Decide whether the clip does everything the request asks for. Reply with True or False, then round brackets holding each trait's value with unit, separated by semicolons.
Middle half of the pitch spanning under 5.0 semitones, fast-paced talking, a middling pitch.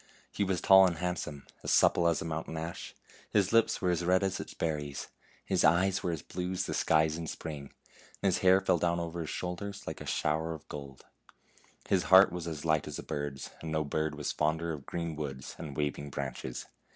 False (3.0 semitones; 220 wpm; 80 Hz)